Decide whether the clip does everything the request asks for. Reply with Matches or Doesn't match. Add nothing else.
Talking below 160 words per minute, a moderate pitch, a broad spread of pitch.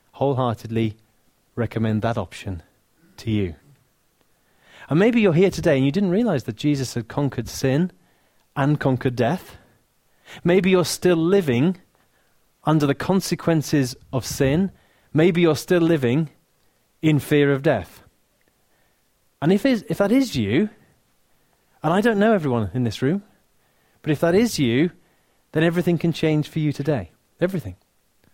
Matches